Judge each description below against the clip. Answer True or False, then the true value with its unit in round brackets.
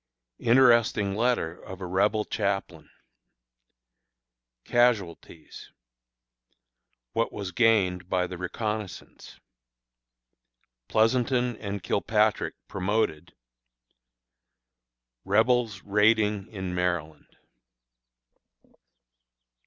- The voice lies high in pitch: False (105 Hz)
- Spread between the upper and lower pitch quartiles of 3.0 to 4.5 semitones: True (3.6 semitones)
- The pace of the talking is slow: True (65 wpm)